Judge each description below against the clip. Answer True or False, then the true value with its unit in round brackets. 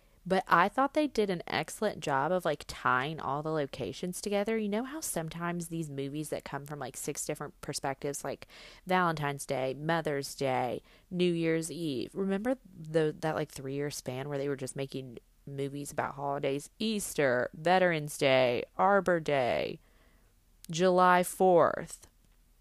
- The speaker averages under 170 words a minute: True (155 wpm)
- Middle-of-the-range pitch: True (155 Hz)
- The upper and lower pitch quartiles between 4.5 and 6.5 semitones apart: True (4.8 semitones)